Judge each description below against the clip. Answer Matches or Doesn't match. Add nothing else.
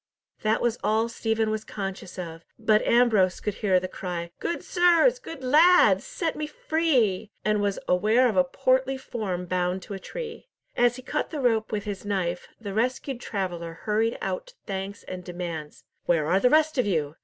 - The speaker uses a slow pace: Doesn't match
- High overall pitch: Matches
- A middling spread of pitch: Doesn't match